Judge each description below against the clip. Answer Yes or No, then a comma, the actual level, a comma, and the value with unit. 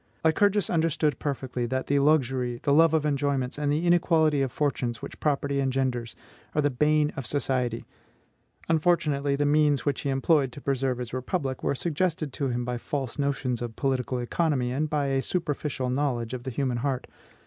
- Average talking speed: Yes, average, 180 wpm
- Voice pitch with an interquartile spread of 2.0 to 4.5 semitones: Yes, average, 2.8 semitones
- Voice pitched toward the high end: No, medium, 140 Hz